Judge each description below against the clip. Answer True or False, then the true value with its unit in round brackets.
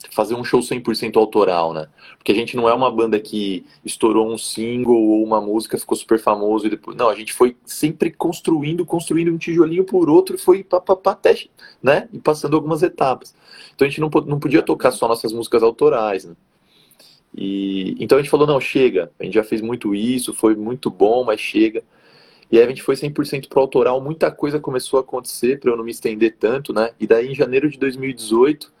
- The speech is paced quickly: True (210 wpm)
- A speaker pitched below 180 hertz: True (135 Hz)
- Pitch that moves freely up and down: True (7.1 semitones)